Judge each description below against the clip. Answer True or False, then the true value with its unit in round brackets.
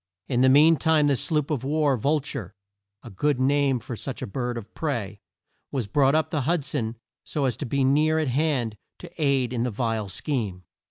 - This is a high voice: False (135 Hz)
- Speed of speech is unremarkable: False (210 wpm)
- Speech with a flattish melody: False (3.9 semitones)